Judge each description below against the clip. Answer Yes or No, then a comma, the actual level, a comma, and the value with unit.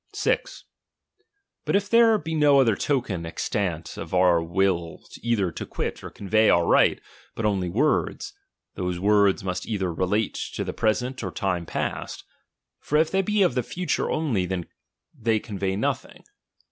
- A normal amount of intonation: No, wide, 6.6 semitones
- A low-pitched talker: Yes, low, 105 Hz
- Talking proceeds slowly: No, average, 160 wpm